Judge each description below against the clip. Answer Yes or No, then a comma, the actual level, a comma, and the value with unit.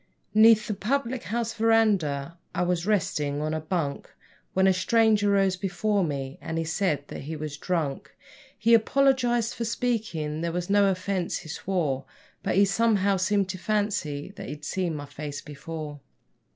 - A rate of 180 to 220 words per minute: No, average, 165 wpm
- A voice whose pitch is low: No, medium, 185 Hz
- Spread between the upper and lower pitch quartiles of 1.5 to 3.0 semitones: No, wide, 5.6 semitones